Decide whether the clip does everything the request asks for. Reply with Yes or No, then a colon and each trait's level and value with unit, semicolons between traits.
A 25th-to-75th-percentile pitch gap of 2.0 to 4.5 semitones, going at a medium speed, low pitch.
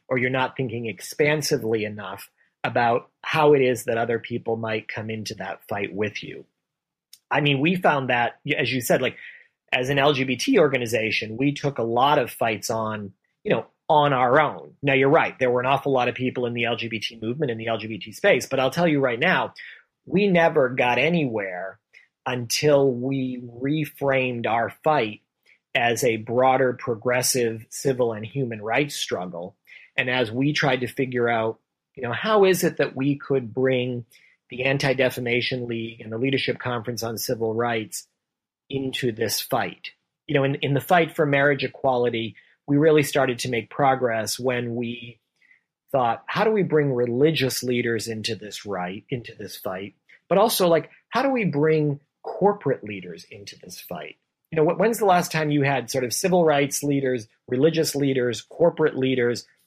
Yes: average, 3.5 semitones; average, 175 wpm; low, 130 Hz